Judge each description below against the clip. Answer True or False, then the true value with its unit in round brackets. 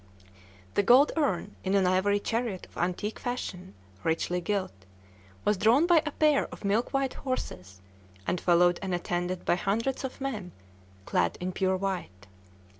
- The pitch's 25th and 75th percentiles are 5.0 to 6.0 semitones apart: True (5.5 semitones)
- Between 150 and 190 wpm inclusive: True (155 wpm)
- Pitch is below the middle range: False (195 Hz)